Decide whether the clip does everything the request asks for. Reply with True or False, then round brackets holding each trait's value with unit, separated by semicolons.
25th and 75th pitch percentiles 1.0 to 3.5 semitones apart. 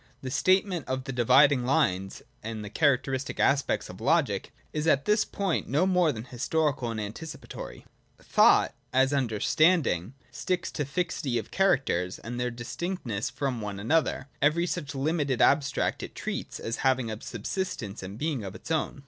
False (5.5 semitones)